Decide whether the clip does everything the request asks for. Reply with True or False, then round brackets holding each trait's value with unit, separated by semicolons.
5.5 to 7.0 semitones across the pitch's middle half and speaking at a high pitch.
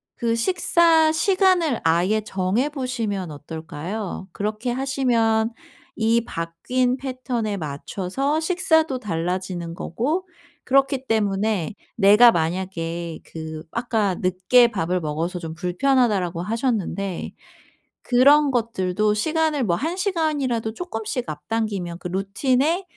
True (6.7 semitones; 220 Hz)